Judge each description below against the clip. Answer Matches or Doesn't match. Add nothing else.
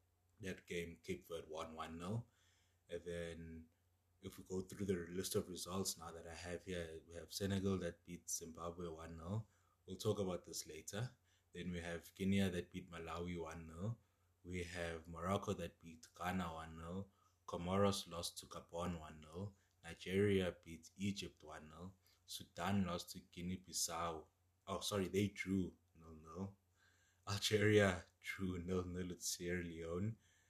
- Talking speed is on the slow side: Doesn't match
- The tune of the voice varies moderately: Doesn't match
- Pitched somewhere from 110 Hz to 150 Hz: Doesn't match